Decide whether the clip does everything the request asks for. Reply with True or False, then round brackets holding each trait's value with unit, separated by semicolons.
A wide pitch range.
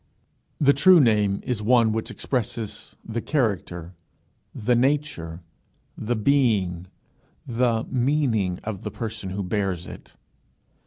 False (4.4 semitones)